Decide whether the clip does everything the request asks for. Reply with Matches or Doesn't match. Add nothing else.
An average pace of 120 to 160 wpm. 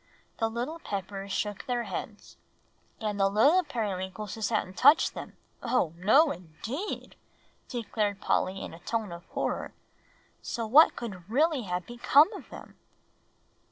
Matches